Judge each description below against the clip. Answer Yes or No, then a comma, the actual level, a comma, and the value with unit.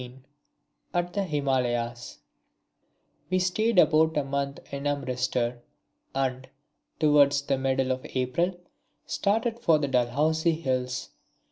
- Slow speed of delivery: Yes, slow, 115 wpm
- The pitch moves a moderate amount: Yes, average, 3.9 semitones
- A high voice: No, medium, 140 Hz